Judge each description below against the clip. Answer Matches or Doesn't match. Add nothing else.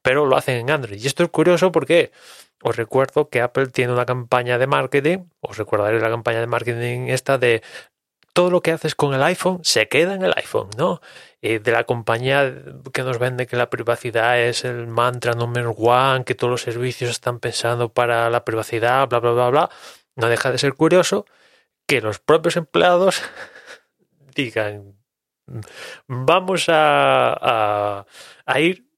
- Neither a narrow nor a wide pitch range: Matches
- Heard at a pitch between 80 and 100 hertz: Doesn't match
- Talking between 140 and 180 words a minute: Matches